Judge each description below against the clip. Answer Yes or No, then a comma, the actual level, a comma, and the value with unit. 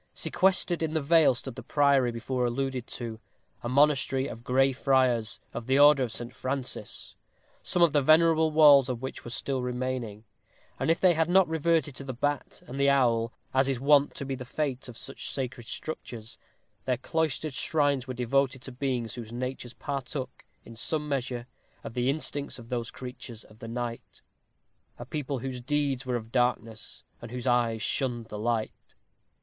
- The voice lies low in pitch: Yes, low, 130 Hz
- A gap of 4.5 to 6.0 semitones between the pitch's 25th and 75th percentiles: No, average, 2.9 semitones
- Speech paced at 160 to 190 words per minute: Yes, average, 180 wpm